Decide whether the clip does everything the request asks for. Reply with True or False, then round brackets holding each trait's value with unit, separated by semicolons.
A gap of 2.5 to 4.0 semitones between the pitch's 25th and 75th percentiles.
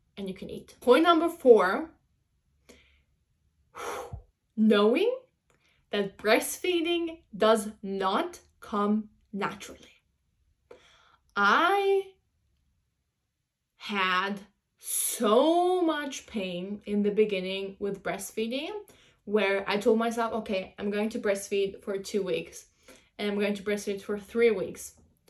False (5.2 semitones)